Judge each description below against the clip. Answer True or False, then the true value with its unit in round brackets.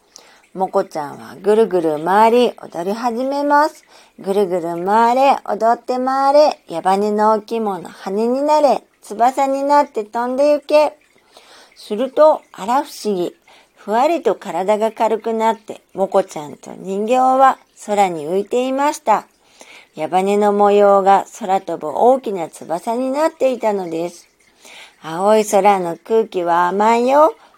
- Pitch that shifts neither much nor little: True (5.0 semitones)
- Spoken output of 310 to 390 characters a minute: False (265 characters per minute)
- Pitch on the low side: False (215 Hz)